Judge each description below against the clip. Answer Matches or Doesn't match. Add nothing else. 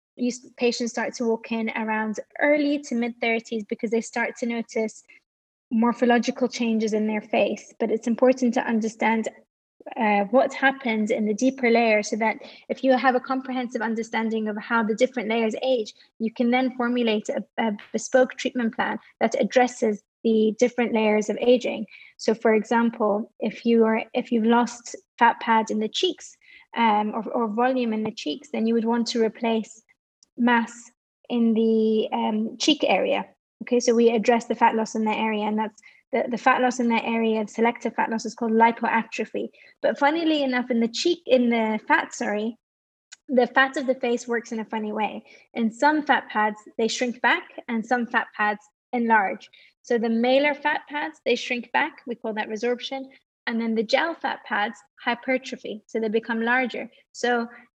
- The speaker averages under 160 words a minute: Doesn't match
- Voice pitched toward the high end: Matches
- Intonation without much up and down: Matches